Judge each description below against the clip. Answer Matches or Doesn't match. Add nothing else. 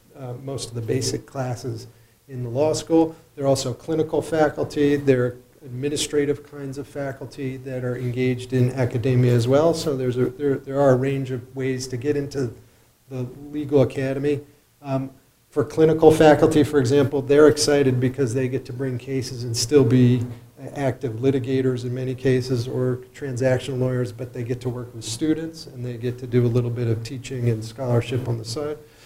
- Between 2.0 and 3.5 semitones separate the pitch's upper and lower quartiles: Matches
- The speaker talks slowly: Doesn't match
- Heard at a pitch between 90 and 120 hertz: Doesn't match